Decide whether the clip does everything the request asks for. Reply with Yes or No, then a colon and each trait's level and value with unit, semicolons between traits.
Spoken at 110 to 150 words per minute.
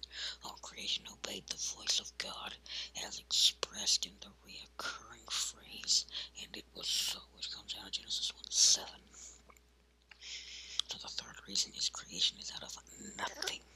Yes: average, 140 wpm